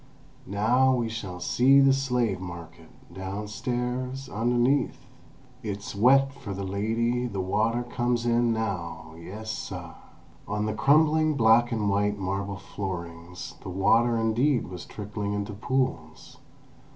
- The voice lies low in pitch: Yes, low, 110 Hz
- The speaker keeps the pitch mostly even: No, average, 3.8 semitones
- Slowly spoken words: Yes, slow, 125 wpm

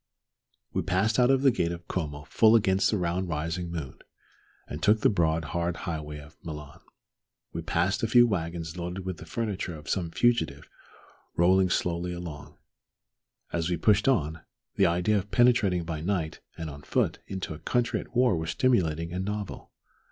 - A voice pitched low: Yes, very low, 90 Hz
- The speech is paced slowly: No, average, 175 wpm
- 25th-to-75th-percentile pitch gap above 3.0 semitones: Yes, average, 3.9 semitones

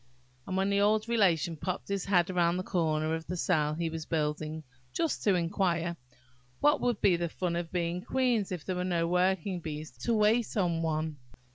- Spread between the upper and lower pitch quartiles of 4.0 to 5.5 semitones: No, average, 3.2 semitones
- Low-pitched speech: No, medium, 175 Hz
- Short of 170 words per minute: No, average, 195 wpm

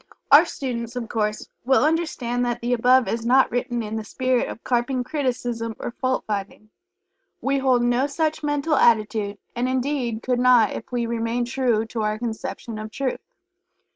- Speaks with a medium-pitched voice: No, high, 245 Hz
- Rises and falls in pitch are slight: Yes, narrow, 2.2 semitones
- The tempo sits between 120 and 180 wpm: Yes, average, 170 wpm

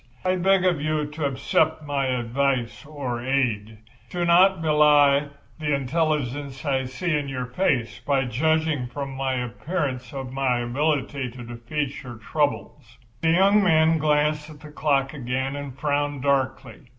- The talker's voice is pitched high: No, medium, 140 Hz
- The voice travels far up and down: No, average, 3.0 semitones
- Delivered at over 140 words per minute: Yes, average, 150 wpm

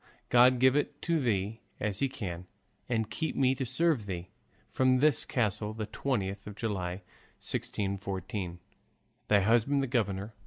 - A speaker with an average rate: Yes, average, 150 wpm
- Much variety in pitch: No, average, 4.7 semitones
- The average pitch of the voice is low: Yes, low, 110 Hz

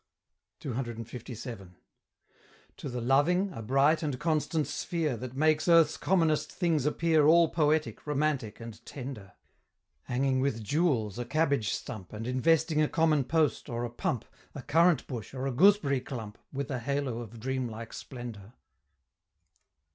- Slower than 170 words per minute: Yes, average, 140 wpm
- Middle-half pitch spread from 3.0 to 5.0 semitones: Yes, average, 4.7 semitones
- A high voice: No, low, 135 Hz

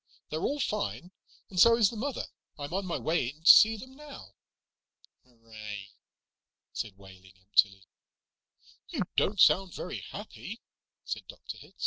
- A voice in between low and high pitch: Yes, medium, 170 Hz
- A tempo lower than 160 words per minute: Yes, average, 145 wpm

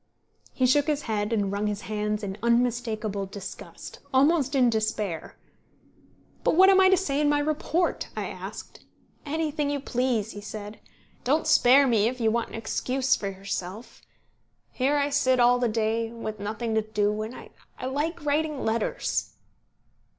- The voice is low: No, high, 235 Hz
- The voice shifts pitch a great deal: No, average, 4.9 semitones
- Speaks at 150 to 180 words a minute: Yes, average, 165 wpm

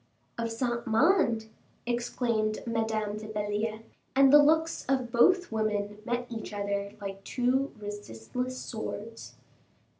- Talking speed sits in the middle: No, slow, 120 wpm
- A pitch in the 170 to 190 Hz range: No, high, 225 Hz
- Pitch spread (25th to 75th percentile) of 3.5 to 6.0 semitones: No, average, 3.0 semitones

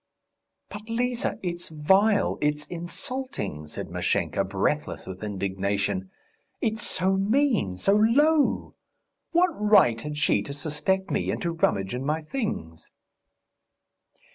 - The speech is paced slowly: Yes, slow, 120 wpm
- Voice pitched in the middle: Yes, medium, 175 Hz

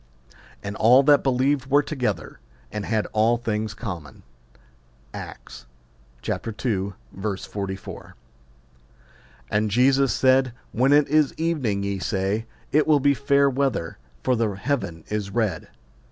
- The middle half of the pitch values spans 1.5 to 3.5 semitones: No, wide, 5.4 semitones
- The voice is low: Yes, low, 115 Hz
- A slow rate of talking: Yes, slow, 125 wpm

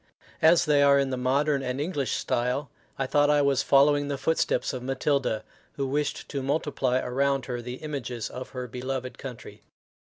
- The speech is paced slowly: No, average, 175 wpm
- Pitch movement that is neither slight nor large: No, narrow, 2.2 semitones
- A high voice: No, low, 135 Hz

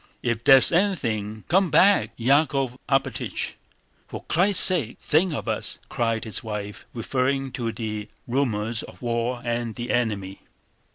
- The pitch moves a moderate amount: Yes, average, 3.8 semitones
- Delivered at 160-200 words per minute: No, average, 145 wpm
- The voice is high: No, low, 120 Hz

